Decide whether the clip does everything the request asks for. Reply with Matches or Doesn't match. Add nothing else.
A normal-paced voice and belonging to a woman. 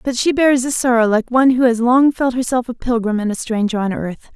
Doesn't match